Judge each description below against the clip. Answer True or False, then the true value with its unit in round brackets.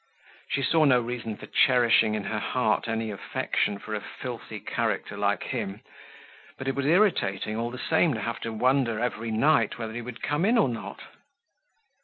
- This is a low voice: True (115 Hz)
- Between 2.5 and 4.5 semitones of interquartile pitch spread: True (3.2 semitones)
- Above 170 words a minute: True (185 wpm)